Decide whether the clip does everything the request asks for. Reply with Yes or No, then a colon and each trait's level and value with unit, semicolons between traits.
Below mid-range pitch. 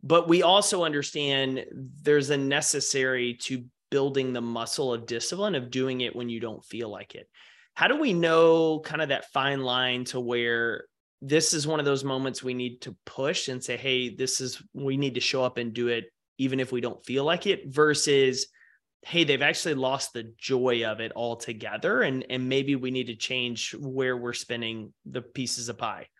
Yes: low, 130 Hz